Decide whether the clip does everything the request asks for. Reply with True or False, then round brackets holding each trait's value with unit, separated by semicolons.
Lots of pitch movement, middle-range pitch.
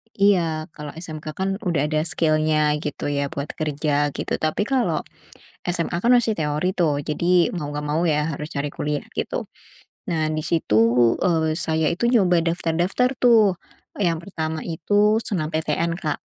False (3.1 semitones; 160 Hz)